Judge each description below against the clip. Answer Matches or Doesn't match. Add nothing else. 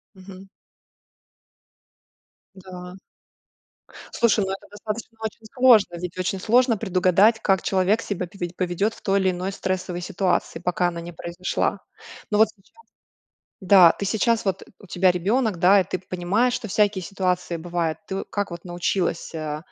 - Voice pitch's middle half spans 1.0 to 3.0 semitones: Matches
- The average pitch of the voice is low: Doesn't match